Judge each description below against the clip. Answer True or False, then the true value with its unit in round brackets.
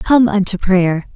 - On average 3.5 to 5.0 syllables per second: True (3.8 syllables/s)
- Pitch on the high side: True (200 Hz)